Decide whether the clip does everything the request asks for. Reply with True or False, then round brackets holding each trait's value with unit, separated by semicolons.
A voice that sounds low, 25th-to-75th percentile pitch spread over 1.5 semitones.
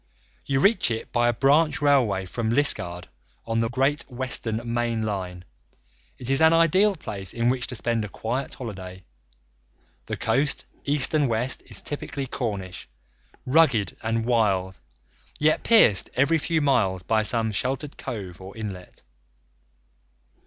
True (120 Hz; 5.2 semitones)